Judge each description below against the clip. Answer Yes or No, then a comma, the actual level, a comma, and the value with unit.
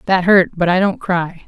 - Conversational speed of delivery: No, fast, 245 wpm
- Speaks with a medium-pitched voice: Yes, medium, 180 Hz